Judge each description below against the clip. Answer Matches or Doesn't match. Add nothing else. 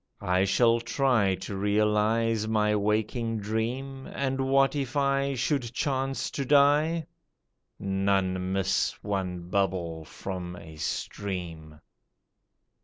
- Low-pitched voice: Matches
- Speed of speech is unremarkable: Doesn't match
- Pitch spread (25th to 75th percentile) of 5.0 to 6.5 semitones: Matches